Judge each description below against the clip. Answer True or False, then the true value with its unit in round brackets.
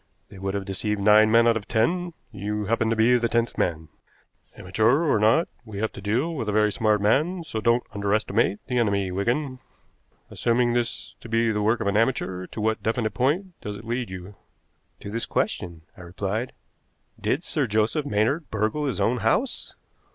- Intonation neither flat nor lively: True (3.1 semitones)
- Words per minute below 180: False (190 wpm)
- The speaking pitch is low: True (110 Hz)